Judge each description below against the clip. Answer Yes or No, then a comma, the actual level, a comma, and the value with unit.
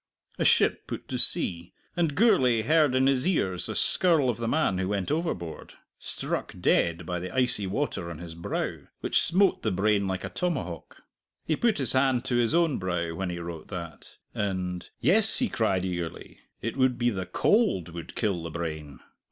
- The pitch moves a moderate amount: No, wide, 7.8 semitones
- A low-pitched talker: Yes, low, 105 Hz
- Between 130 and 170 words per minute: No, average, 190 wpm